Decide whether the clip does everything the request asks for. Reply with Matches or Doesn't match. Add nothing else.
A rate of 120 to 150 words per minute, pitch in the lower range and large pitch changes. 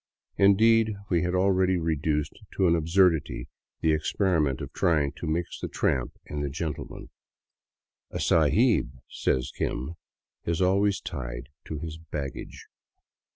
Doesn't match